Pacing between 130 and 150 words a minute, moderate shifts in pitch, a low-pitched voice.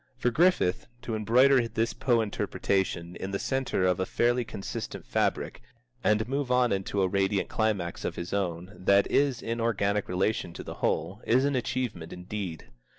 No: average, 170 wpm; average, 4.6 semitones; low, 105 Hz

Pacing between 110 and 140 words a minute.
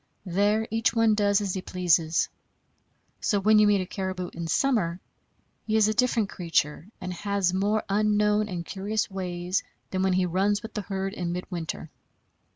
No: average, 170 wpm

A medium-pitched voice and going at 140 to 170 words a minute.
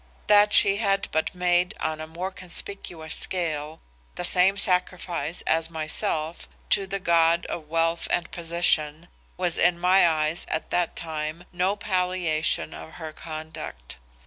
Yes: medium, 170 Hz; average, 145 wpm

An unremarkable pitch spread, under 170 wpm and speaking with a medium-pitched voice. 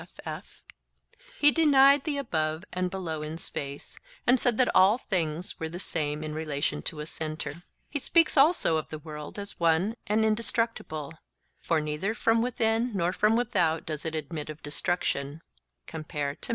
No: wide, 6.6 semitones; average, 160 wpm; medium, 170 Hz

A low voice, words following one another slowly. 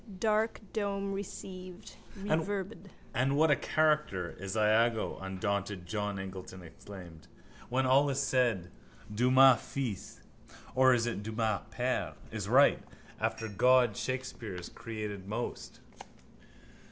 Yes: low, 120 Hz; slow, 115 wpm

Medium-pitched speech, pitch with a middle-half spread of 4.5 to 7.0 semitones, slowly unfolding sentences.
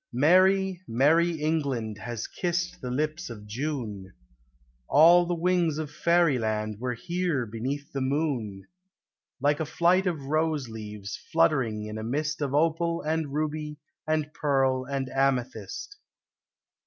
Yes: medium, 145 Hz; average, 5.0 semitones; slow, 130 wpm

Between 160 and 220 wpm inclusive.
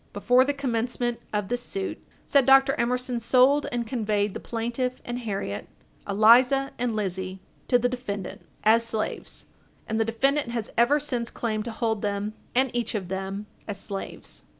Yes: average, 165 wpm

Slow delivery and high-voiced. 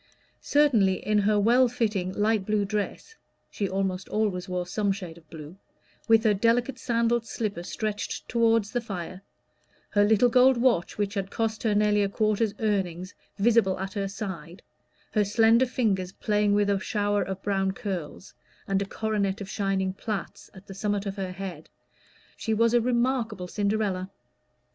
No: average, 165 wpm; high, 205 Hz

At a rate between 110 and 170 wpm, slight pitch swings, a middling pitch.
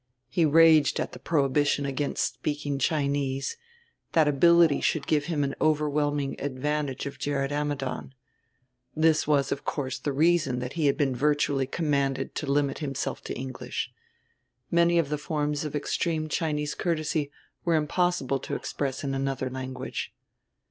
Yes: average, 150 wpm; narrow, 2.1 semitones; medium, 145 Hz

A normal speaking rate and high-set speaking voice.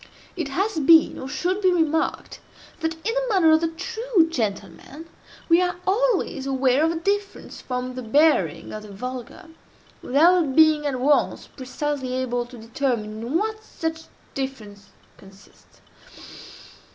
Yes: average, 150 wpm; very high, 295 Hz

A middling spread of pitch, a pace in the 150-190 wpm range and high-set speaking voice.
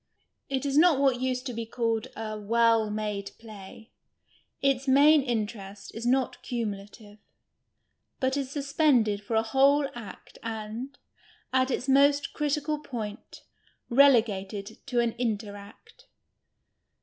No: average, 4.2 semitones; slow, 135 wpm; high, 240 Hz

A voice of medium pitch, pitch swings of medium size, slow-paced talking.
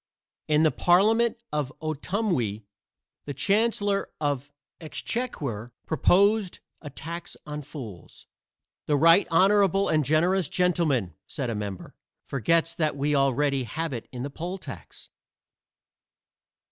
Yes: medium, 155 Hz; average, 4.9 semitones; slow, 120 wpm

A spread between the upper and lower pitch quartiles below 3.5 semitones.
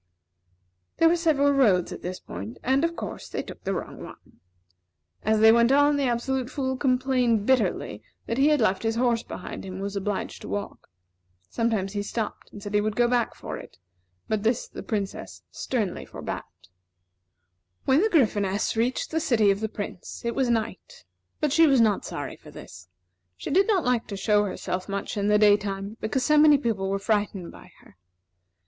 No: average, 4.7 semitones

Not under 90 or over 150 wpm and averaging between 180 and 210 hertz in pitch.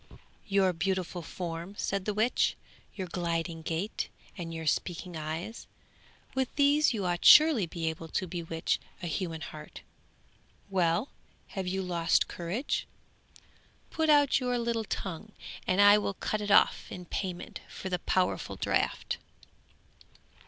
Yes: average, 140 wpm; medium, 185 Hz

